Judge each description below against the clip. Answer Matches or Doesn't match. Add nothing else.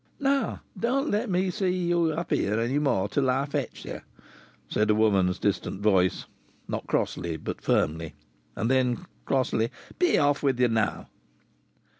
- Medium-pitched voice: Doesn't match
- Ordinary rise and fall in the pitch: Doesn't match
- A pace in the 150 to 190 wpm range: Matches